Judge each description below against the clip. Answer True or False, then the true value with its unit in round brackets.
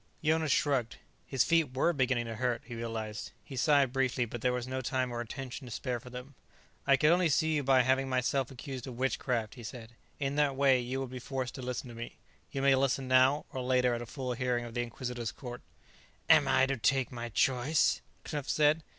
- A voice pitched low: True (130 Hz)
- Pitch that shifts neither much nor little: False (2.0 semitones)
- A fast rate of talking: True (225 wpm)